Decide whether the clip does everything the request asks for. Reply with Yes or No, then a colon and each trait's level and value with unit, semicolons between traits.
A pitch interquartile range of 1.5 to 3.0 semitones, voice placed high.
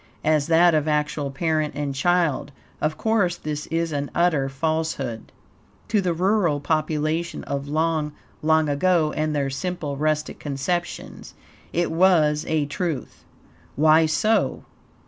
No: narrow, 2.6 semitones; medium, 155 Hz